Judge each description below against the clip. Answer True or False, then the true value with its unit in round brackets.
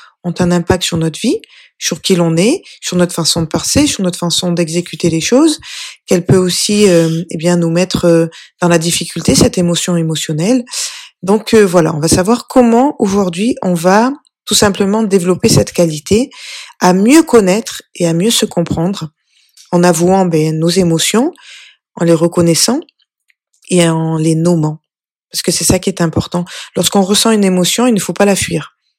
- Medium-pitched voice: True (180 Hz)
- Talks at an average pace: True (180 wpm)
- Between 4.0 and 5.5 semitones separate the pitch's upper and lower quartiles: True (4.3 semitones)